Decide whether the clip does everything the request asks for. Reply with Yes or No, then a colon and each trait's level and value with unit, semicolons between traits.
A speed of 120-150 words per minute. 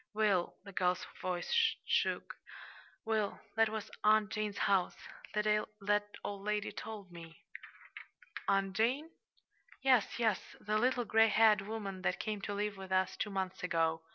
Yes: average, 145 wpm